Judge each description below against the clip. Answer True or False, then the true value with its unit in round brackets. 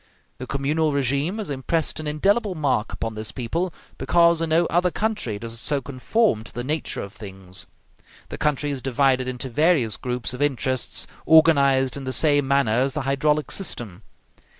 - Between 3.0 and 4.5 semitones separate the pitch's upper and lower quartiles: True (4.1 semitones)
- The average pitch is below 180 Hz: True (140 Hz)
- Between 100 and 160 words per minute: False (175 wpm)